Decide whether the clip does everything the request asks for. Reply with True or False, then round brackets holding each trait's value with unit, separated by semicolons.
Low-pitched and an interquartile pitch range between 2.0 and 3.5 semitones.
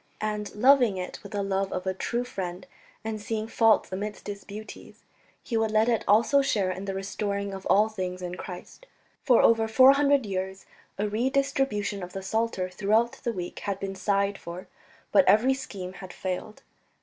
False (205 Hz; 2.9 semitones)